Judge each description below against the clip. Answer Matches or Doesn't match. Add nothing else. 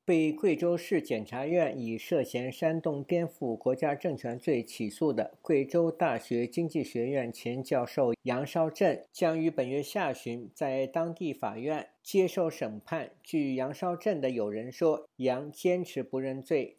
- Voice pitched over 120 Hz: Matches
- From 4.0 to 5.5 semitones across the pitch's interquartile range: Matches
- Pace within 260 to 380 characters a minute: Doesn't match